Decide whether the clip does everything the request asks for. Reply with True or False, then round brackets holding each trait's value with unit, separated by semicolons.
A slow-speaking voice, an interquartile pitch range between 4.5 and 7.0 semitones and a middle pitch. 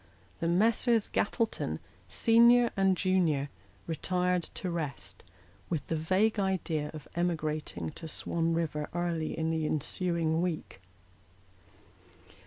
False (110 wpm; 3.1 semitones; 170 Hz)